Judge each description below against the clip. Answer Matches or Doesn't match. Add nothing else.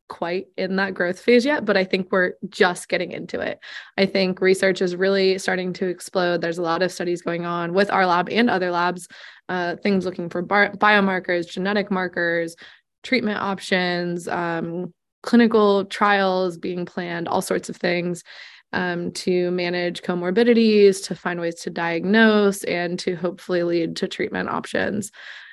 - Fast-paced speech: Doesn't match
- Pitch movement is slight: Matches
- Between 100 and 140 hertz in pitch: Doesn't match